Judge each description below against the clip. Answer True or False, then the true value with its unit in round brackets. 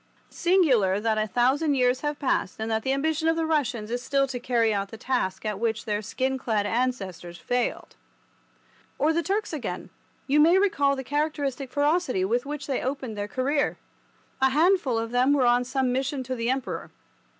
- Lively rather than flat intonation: False (4.1 semitones)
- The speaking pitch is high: True (260 Hz)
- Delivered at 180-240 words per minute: True (190 wpm)